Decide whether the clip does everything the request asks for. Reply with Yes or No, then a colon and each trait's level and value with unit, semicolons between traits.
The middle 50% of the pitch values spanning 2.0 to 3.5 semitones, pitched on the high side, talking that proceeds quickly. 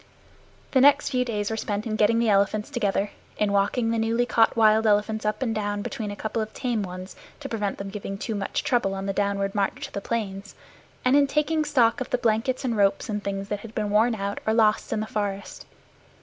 Yes: narrow, 2.5 semitones; high, 215 Hz; fast, 230 wpm